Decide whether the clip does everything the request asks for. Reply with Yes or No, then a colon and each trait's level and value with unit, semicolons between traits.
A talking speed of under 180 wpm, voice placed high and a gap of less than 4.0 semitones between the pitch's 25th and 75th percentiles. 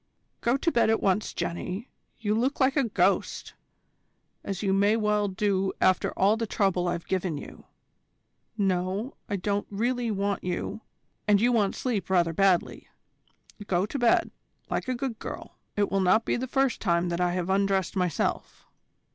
Yes: average, 170 wpm; high, 200 Hz; average, 3.4 semitones